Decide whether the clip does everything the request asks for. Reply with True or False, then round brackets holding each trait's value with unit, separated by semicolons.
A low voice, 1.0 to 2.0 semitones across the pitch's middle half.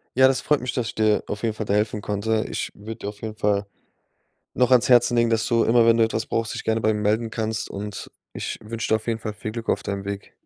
True (110 Hz; 1.7 semitones)